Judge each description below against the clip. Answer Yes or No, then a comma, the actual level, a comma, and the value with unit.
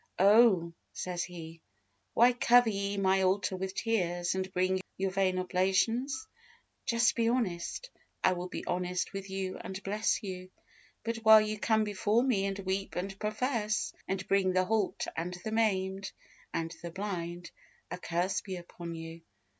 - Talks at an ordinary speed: Yes, average, 160 wpm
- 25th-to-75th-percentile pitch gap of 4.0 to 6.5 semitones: No, average, 2.8 semitones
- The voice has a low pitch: No, high, 190 Hz